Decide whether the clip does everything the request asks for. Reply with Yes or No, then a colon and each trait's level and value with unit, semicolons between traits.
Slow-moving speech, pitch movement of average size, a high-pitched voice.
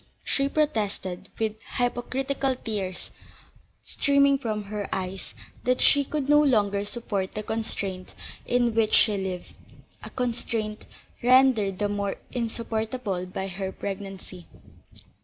Yes: slow, 120 wpm; average, 4.2 semitones; high, 215 Hz